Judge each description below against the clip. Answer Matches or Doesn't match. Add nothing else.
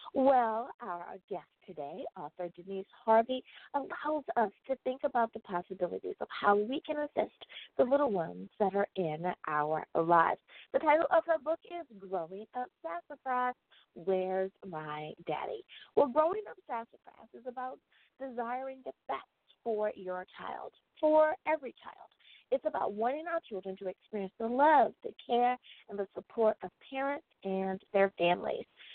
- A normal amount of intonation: Doesn't match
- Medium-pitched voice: Doesn't match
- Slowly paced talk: Doesn't match